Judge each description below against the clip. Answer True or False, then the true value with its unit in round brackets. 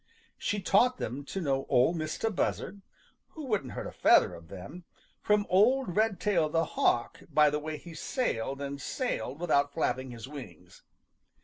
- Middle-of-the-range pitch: True (155 Hz)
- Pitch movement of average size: False (6.7 semitones)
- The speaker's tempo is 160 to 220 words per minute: True (165 wpm)